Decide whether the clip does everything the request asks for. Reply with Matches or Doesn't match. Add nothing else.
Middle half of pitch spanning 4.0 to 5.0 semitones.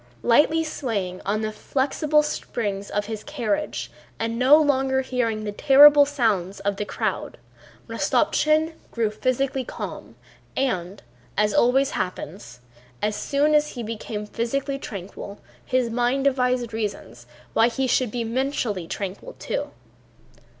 Matches